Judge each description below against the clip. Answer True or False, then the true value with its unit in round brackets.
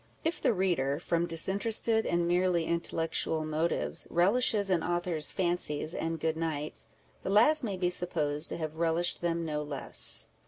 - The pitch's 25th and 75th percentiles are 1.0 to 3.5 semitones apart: True (2.6 semitones)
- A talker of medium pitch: True (170 Hz)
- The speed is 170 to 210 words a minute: False (160 wpm)